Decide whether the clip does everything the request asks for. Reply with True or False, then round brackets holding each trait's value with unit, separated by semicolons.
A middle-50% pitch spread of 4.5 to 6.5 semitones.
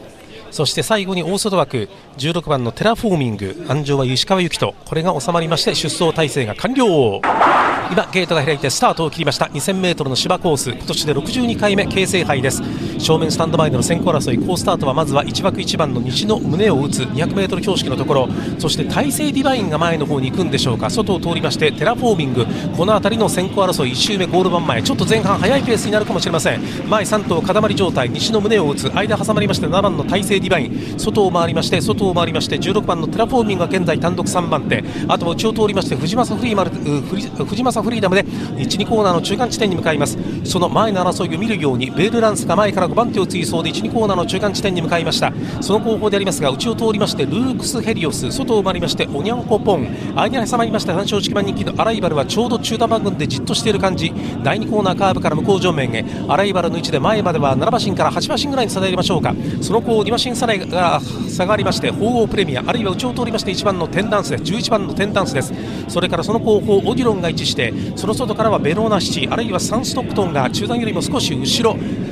True (5.4 semitones)